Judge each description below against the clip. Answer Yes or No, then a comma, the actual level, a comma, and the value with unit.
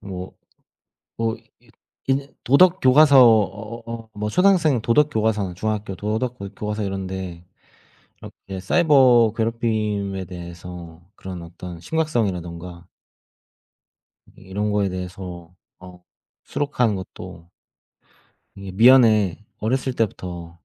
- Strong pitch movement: No, average, 4.4 semitones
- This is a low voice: Yes, low, 105 Hz